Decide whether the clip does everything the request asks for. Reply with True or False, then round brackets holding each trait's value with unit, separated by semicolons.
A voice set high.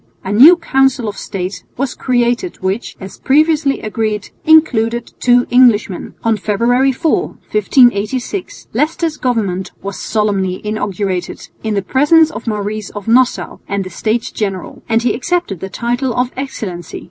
True (230 Hz)